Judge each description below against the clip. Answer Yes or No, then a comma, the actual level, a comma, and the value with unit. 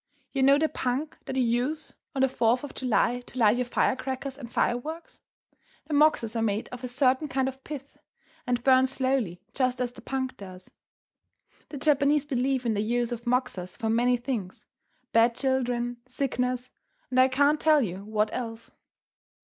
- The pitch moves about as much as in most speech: No, narrow, 2.1 semitones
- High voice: Yes, very high, 250 Hz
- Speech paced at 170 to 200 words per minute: Yes, average, 175 wpm